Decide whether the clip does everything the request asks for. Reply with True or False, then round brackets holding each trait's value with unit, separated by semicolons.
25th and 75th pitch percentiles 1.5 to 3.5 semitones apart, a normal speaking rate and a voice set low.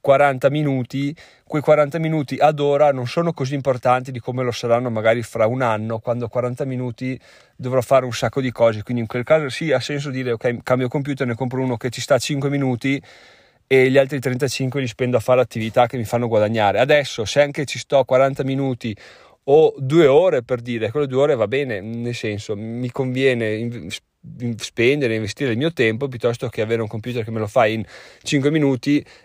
False (3.0 semitones; 200 wpm; 130 Hz)